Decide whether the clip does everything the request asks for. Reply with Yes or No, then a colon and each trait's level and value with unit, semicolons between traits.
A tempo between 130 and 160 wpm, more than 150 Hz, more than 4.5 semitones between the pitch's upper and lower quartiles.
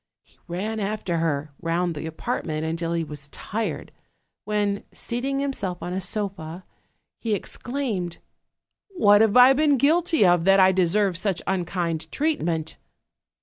Yes: average, 145 wpm; high, 190 Hz; average, 4.9 semitones